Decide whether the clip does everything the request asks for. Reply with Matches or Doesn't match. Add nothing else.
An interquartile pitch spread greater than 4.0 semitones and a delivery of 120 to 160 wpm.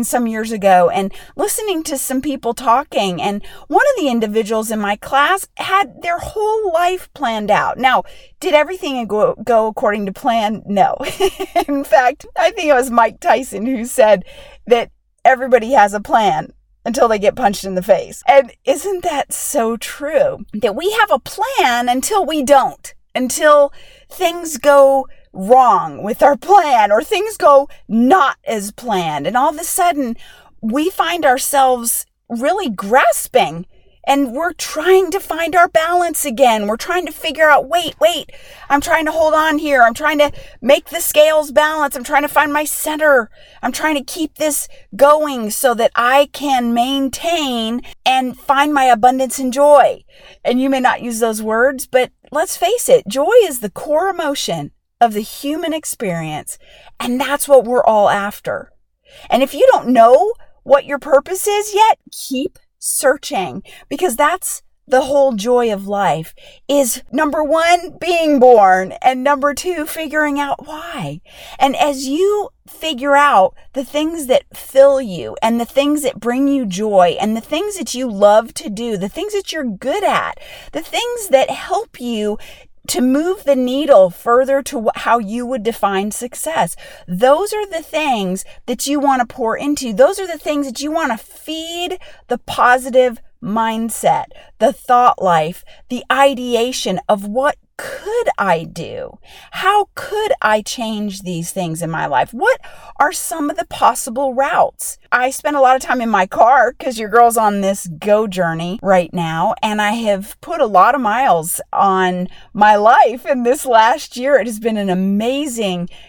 Doesn't match